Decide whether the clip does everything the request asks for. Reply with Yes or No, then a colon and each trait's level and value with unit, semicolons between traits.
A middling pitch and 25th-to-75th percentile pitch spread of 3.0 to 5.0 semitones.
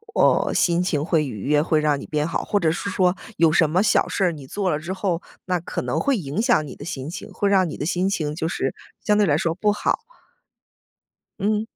Yes: medium, 170 Hz; average, 4.2 semitones